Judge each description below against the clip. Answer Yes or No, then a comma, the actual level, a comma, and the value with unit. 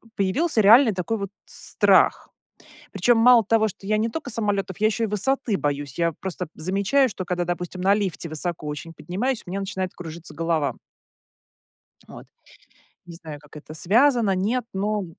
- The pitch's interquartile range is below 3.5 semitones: No, average, 4.5 semitones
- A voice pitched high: Yes, high, 195 Hz